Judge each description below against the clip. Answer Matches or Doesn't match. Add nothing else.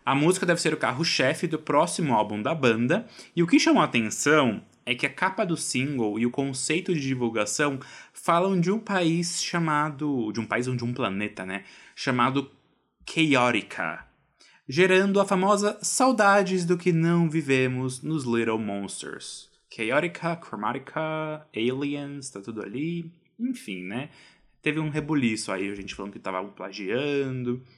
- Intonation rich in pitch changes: Matches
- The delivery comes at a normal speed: Matches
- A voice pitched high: Doesn't match